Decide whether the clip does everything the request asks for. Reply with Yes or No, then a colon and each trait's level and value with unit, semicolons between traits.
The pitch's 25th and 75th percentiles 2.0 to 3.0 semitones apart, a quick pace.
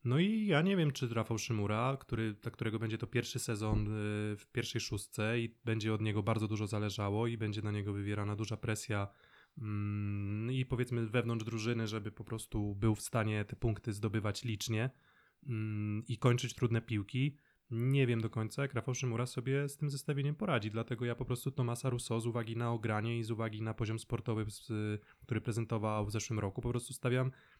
Yes: narrow, 2.4 semitones; fast, 190 wpm